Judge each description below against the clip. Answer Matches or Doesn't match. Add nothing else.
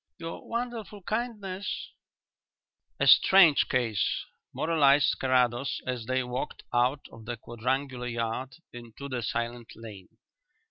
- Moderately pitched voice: Doesn't match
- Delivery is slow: Matches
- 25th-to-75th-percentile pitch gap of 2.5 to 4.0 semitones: Doesn't match